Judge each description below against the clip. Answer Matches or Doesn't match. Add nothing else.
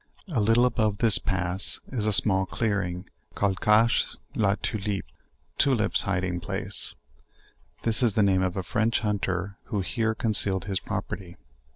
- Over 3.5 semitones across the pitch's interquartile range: Doesn't match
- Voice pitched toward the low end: Matches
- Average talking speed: Matches